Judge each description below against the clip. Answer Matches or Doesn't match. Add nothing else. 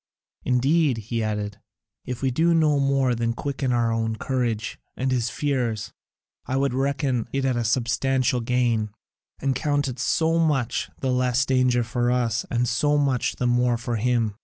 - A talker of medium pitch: Doesn't match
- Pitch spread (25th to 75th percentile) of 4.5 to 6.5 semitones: Doesn't match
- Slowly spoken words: Doesn't match